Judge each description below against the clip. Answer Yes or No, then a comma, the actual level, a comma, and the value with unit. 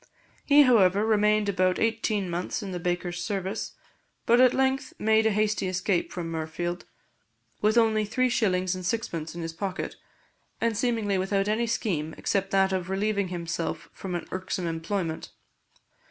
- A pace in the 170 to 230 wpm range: No, average, 155 wpm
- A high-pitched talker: Yes, high, 195 Hz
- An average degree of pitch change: Yes, average, 3.5 semitones